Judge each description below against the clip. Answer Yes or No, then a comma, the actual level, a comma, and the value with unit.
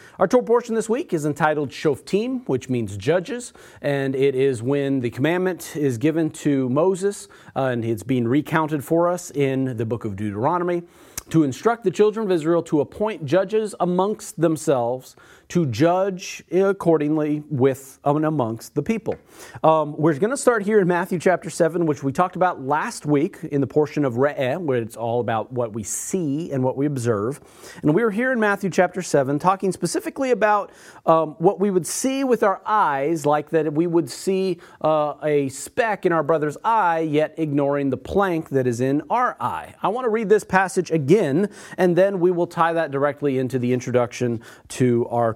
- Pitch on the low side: No, medium, 160 Hz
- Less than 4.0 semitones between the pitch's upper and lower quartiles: No, average, 5.3 semitones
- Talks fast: No, average, 190 wpm